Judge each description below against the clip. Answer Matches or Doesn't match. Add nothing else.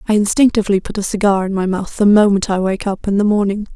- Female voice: Matches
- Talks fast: Matches